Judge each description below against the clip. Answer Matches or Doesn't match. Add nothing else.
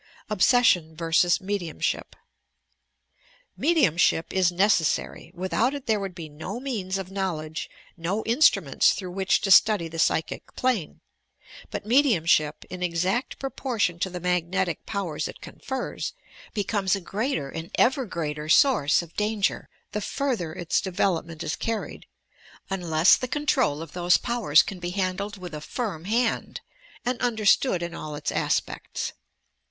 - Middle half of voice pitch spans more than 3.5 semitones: Matches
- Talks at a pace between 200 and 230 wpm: Doesn't match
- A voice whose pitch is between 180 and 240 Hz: Matches